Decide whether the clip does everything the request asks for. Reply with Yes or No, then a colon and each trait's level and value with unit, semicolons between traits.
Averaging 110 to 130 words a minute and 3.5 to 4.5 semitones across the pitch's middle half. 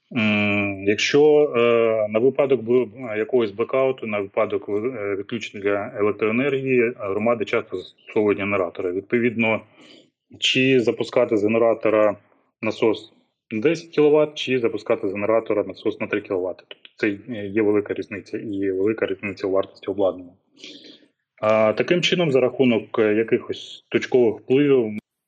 Yes: average, 120 wpm; average, 3.8 semitones